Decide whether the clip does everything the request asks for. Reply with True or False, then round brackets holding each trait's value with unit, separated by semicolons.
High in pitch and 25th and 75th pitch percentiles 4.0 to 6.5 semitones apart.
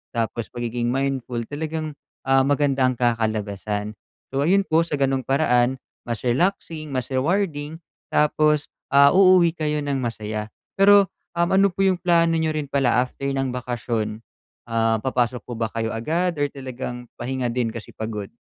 False (135 Hz; 4.7 semitones)